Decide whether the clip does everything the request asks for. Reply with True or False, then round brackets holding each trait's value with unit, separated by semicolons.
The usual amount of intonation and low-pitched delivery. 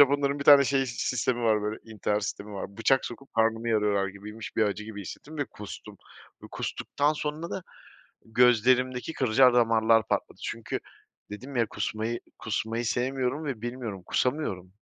True (3.7 semitones; 115 Hz)